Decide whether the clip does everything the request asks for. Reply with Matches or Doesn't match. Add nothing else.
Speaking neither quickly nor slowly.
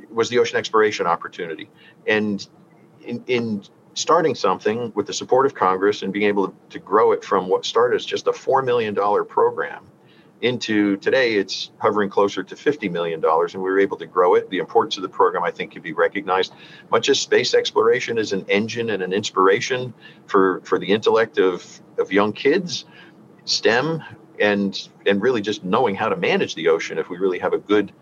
Matches